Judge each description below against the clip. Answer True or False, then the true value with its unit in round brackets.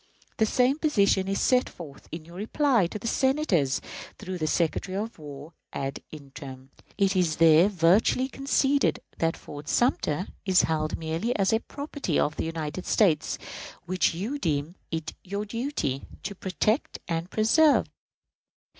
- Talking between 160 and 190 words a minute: False (145 wpm)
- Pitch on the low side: False (185 Hz)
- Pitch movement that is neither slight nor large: False (6.1 semitones)